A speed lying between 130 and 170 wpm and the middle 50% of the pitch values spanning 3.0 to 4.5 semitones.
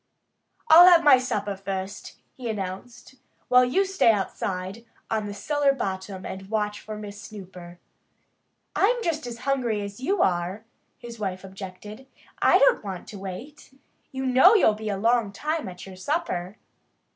No: average, 155 wpm; wide, 5.5 semitones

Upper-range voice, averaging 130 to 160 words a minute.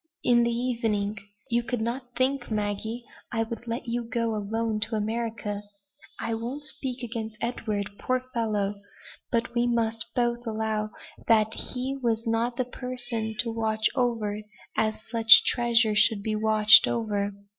Yes: high, 230 Hz; average, 155 wpm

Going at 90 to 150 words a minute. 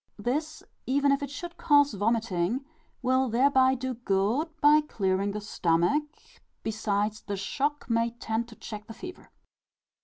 Yes: average, 145 wpm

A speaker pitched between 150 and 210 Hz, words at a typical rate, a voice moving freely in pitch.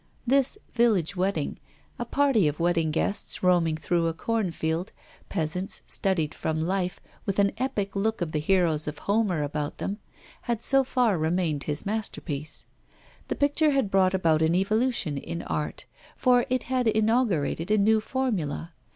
Yes: high, 190 Hz; average, 160 wpm; wide, 5.8 semitones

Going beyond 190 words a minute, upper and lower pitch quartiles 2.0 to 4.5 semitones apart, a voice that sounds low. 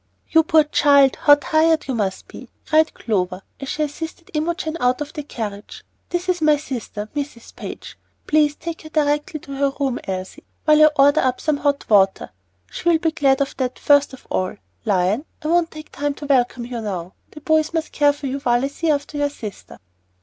No: average, 200 wpm; average, 3.8 semitones; very high, 285 Hz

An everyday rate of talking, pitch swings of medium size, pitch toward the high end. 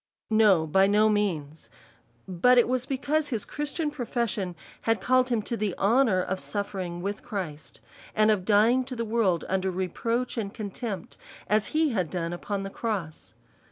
Yes: average, 165 wpm; average, 4.3 semitones; high, 210 Hz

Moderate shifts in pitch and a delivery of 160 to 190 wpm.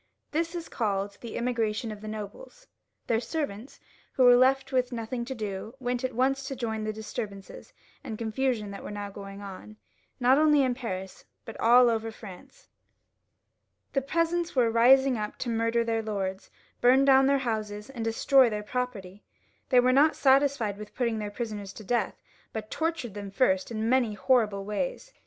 Yes: average, 3.8 semitones; average, 180 wpm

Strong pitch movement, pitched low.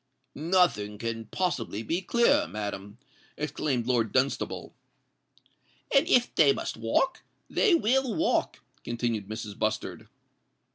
Yes: wide, 9.0 semitones; low, 120 Hz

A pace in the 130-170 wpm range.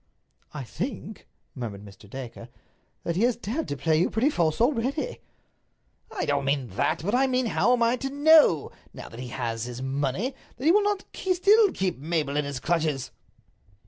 No: average, 185 wpm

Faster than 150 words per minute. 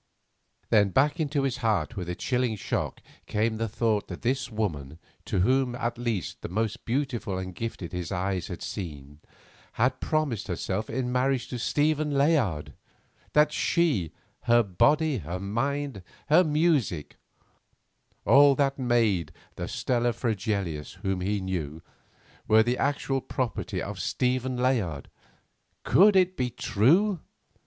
No: slow, 135 wpm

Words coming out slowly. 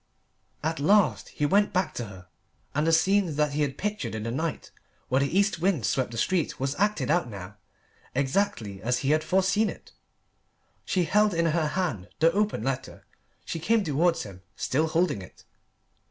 No: average, 185 wpm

